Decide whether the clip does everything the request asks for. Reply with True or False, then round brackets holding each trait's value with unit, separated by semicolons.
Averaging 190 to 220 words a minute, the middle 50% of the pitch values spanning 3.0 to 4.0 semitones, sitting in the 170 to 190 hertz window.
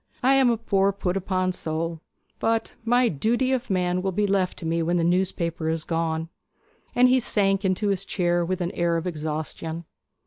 True (195 wpm; 3.4 semitones; 185 Hz)